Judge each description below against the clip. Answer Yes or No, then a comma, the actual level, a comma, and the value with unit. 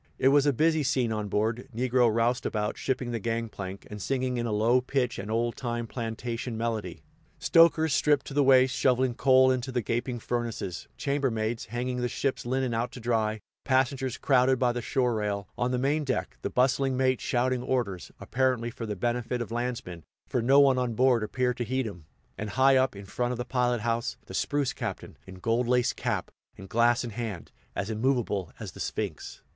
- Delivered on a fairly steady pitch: Yes, narrow, 2.3 semitones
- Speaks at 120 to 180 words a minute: No, average, 200 wpm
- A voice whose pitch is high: No, low, 120 Hz